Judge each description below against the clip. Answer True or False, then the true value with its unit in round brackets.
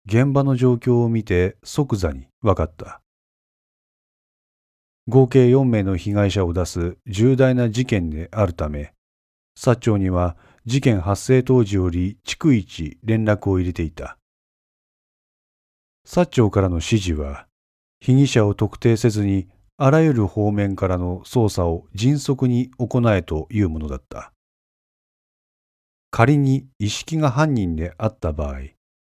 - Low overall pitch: True (100 Hz)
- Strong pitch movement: True (6.4 semitones)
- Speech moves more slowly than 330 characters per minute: True (230 characters per minute)